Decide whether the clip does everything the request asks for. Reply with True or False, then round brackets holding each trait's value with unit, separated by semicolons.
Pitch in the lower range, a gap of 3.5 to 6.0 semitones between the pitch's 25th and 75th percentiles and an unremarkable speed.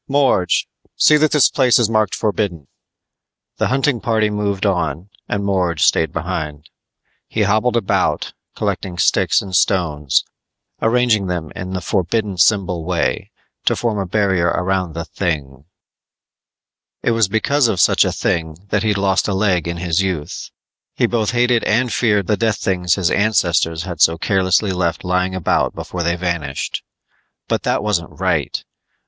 True (95 Hz; 4.0 semitones; 155 wpm)